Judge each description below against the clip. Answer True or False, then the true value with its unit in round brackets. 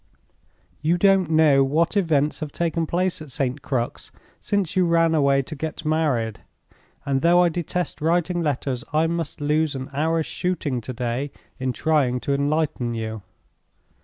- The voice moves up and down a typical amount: True (3.6 semitones)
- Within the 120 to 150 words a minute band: False (160 wpm)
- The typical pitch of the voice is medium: True (155 Hz)